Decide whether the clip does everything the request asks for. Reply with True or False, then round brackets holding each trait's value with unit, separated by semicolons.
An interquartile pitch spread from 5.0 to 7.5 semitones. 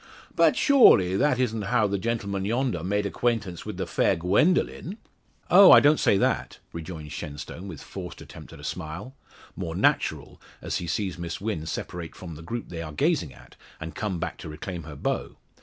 True (5.3 semitones)